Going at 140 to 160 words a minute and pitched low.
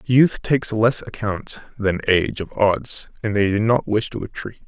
No: average, 190 wpm; low, 110 Hz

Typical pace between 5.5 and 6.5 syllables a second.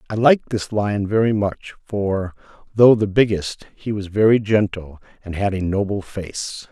No: 4.4 syllables/s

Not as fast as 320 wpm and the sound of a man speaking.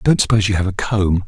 No: fast, 330 wpm; male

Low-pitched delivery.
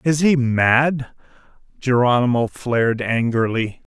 Yes: low, 125 Hz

